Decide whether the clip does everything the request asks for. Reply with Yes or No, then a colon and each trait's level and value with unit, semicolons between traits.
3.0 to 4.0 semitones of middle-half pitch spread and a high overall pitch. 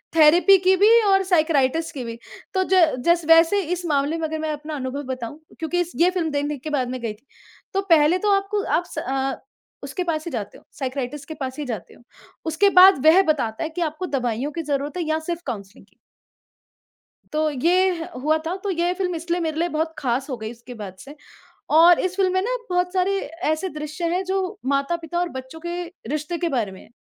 No: average, 4.4 semitones; very high, 315 Hz